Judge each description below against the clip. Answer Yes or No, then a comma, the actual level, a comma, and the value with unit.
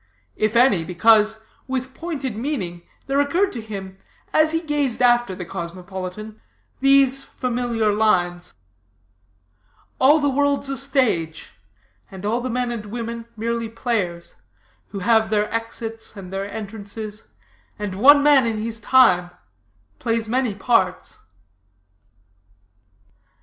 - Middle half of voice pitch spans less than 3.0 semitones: No, average, 4.3 semitones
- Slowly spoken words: Yes, slow, 125 wpm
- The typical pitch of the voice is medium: No, high, 225 Hz